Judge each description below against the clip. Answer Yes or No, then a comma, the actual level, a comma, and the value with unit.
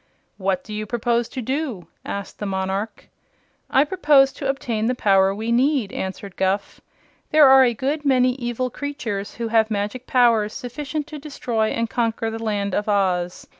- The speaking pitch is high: Yes, high, 230 Hz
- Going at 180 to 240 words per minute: No, average, 170 wpm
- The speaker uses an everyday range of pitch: Yes, average, 4.6 semitones